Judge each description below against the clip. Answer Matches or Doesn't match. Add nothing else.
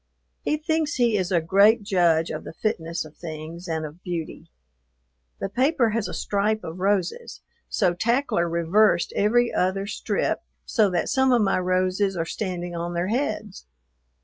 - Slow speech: Doesn't match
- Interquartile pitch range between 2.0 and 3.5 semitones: Doesn't match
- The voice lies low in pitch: Doesn't match